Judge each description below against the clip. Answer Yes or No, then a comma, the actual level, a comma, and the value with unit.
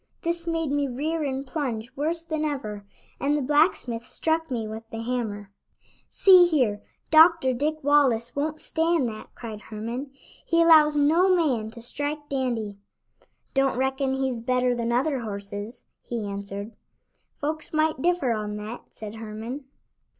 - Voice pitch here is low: No, very high, 265 Hz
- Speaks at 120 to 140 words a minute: No, average, 150 wpm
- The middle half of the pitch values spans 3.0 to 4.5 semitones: No, wide, 5.4 semitones